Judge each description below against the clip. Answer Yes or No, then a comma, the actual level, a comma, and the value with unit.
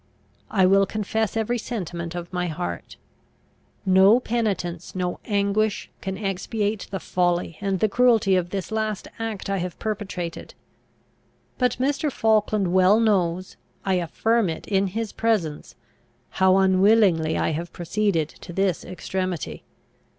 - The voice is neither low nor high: No, high, 195 Hz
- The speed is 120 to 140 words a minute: Yes, slow, 135 wpm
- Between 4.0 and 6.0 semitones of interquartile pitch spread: No, average, 3.4 semitones